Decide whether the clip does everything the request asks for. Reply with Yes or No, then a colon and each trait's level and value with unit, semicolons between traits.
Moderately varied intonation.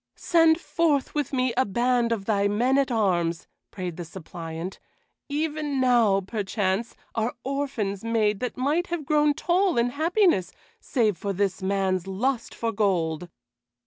No: wide, 6.2 semitones